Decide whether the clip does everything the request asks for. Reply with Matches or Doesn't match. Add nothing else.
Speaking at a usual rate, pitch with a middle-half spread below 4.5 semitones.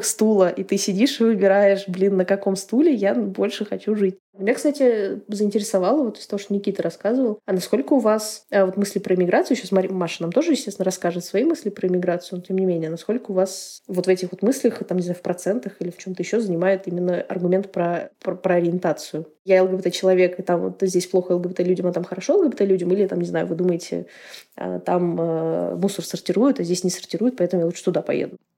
Doesn't match